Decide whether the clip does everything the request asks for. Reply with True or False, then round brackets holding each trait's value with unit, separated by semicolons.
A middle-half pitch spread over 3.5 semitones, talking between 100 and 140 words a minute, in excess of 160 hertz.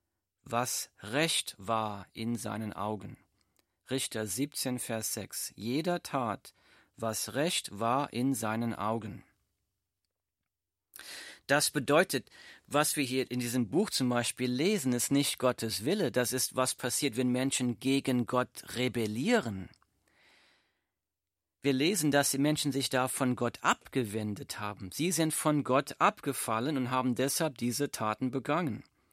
False (4.1 semitones; 130 wpm; 125 Hz)